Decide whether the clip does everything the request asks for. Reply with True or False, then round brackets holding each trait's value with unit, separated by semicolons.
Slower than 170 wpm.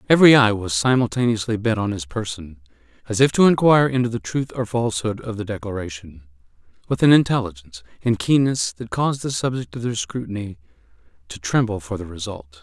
False (175 wpm)